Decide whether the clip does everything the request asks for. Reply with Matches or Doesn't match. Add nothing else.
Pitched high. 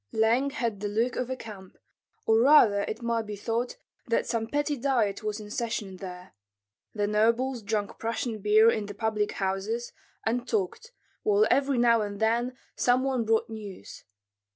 Matches